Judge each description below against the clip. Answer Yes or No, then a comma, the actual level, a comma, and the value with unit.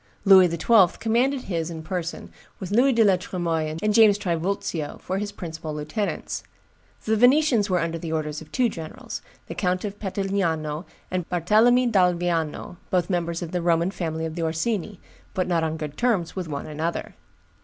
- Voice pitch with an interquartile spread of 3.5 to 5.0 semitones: Yes, average, 4.1 semitones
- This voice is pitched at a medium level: Yes, medium, 180 Hz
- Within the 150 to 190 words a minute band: Yes, average, 175 wpm